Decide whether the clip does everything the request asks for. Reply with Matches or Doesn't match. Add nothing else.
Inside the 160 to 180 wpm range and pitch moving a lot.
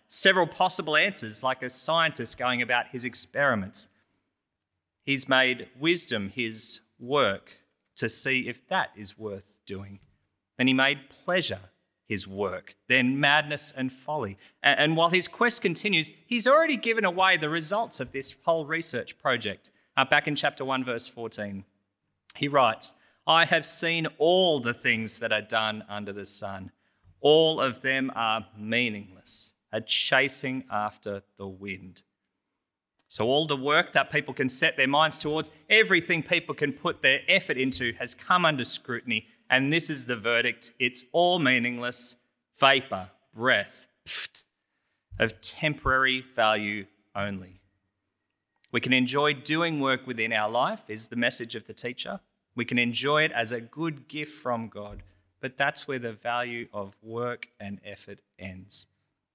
Doesn't match